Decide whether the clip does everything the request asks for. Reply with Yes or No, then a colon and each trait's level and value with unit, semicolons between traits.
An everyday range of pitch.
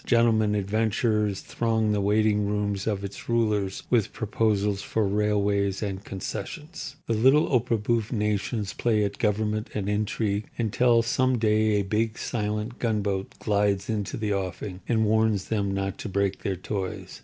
No: narrow, 1.8 semitones